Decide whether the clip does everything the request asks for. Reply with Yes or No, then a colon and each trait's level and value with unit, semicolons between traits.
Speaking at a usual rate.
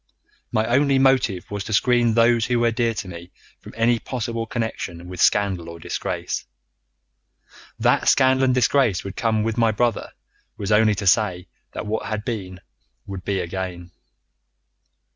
Yes: average, 160 wpm